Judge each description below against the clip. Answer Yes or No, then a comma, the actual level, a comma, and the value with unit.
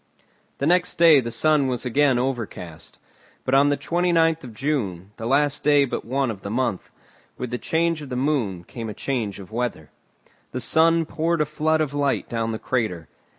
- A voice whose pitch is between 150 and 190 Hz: No, low, 135 Hz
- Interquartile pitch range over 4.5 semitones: Yes, average, 5.0 semitones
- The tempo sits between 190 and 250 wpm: Yes, average, 195 wpm